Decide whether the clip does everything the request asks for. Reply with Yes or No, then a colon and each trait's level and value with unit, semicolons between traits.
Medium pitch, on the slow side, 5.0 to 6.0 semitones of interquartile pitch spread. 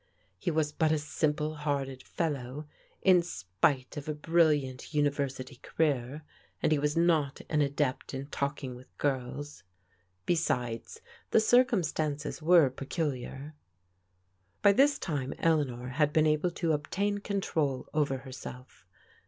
No: medium, 150 Hz; slow, 130 wpm; average, 3.2 semitones